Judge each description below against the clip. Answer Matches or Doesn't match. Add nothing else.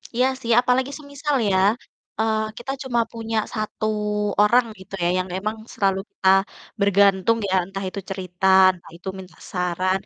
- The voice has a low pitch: Doesn't match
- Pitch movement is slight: Doesn't match